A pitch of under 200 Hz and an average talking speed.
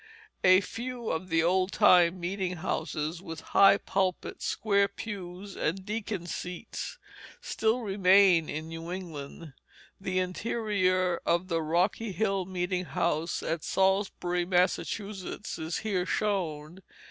No: medium, 185 Hz; slow, 125 wpm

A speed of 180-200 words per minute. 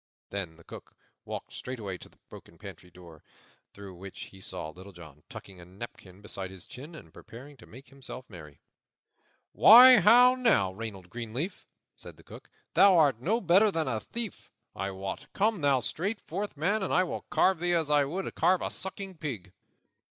Yes: average, 185 wpm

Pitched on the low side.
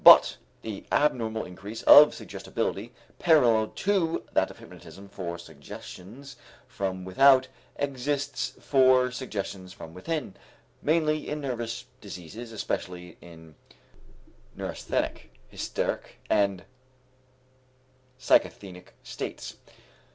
Yes: low, 115 Hz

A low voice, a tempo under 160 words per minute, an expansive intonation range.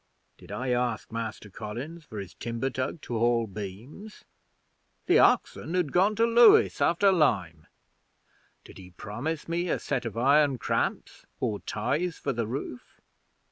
Yes: low, 125 Hz; average, 150 wpm; wide, 6.9 semitones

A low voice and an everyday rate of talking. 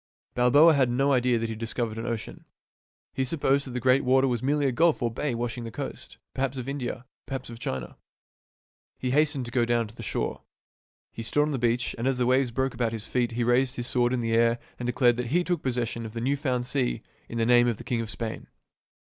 No: low, 125 Hz; fast, 245 wpm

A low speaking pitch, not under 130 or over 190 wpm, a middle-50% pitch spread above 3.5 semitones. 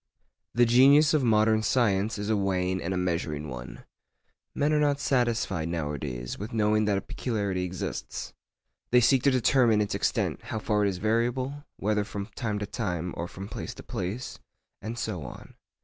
Yes: low, 105 Hz; average, 175 wpm; average, 4.6 semitones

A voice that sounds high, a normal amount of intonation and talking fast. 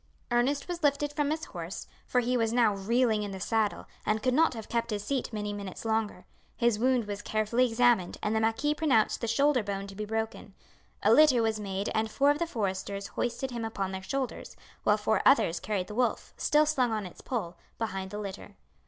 Yes: high, 225 Hz; average, 3.6 semitones; fast, 215 wpm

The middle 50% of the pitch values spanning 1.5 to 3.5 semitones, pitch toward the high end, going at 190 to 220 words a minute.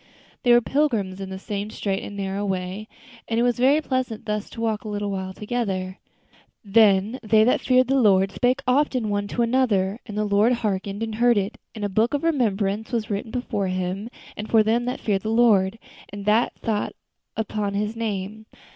Yes: average, 3.1 semitones; high, 215 Hz; average, 195 wpm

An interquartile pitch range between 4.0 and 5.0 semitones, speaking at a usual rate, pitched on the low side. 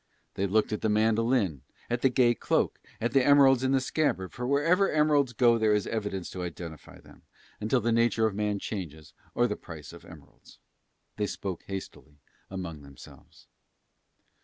Yes: average, 4.6 semitones; average, 170 wpm; low, 110 Hz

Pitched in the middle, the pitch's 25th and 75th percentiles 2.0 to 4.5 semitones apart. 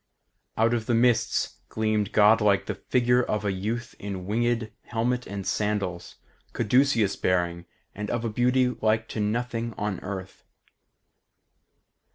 No: low, 110 Hz; average, 2.8 semitones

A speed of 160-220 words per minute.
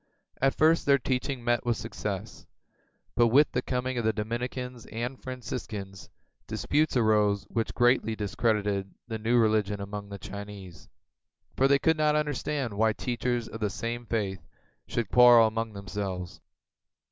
No: average, 145 wpm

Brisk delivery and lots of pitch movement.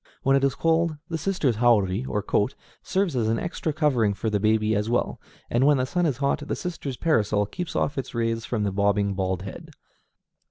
Yes: fast, 210 wpm; wide, 6.2 semitones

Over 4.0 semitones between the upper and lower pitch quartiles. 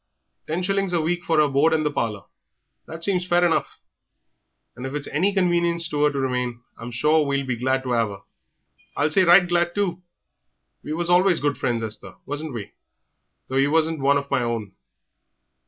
Yes: average, 5.0 semitones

